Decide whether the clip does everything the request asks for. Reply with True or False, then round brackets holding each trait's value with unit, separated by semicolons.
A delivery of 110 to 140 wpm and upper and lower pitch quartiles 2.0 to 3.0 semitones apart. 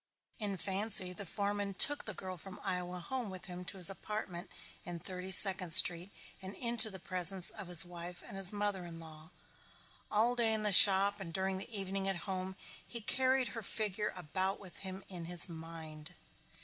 False (190 wpm; 2.4 semitones)